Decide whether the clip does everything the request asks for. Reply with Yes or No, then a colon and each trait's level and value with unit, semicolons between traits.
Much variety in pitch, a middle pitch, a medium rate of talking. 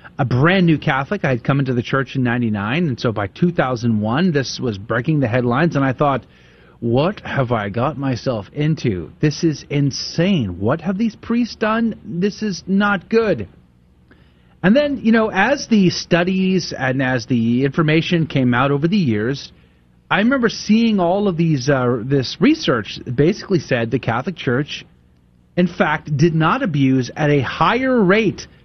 Yes: wide, 7.0 semitones; medium, 145 Hz; average, 170 wpm